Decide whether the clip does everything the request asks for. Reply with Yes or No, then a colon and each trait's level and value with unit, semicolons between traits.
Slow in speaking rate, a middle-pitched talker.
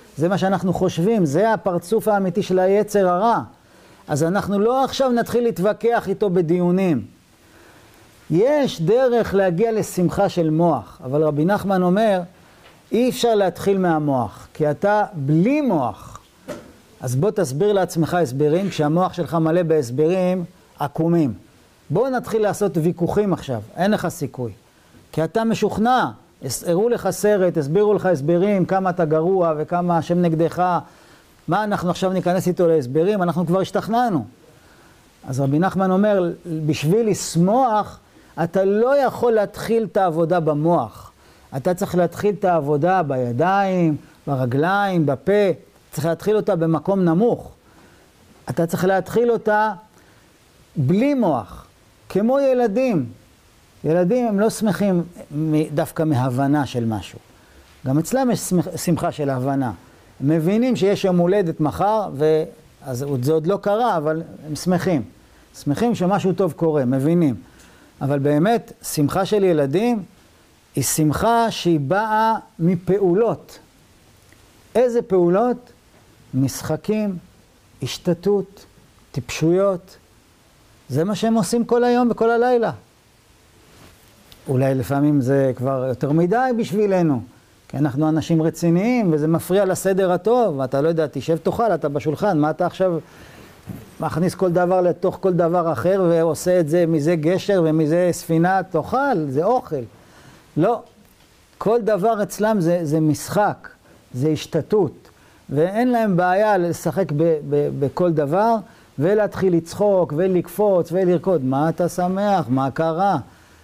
No: average, 125 wpm; medium, 175 Hz